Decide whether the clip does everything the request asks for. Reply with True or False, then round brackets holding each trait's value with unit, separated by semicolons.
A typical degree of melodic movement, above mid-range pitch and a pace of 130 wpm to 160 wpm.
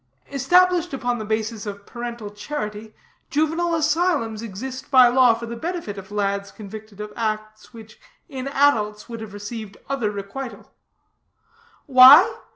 True (4.6 semitones; 230 Hz; 140 wpm)